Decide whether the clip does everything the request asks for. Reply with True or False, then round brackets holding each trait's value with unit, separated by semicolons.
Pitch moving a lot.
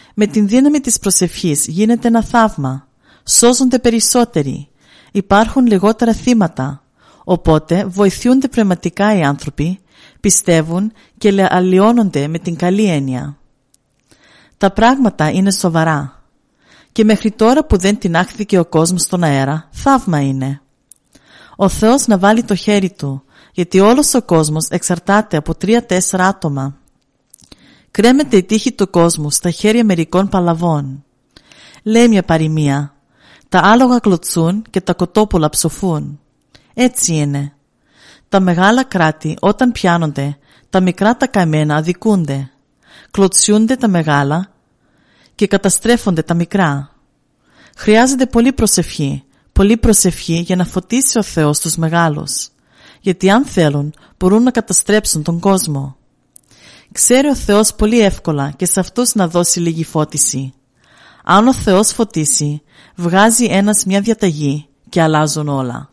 True (5.7 semitones)